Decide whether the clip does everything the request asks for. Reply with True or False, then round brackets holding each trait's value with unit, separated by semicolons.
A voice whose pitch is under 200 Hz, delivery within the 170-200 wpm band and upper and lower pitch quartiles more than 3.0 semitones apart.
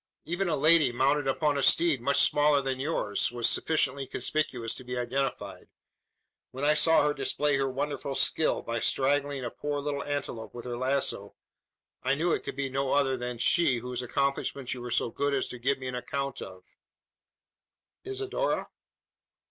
False (135 Hz; 175 wpm; 2.7 semitones)